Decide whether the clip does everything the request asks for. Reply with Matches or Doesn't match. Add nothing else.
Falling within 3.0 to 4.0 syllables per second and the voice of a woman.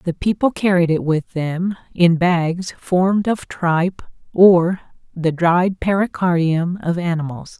Matches